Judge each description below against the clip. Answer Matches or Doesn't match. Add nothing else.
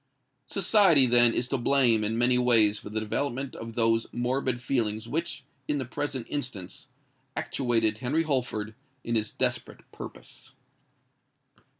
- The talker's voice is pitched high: Doesn't match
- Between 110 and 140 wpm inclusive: Matches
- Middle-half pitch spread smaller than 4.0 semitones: Matches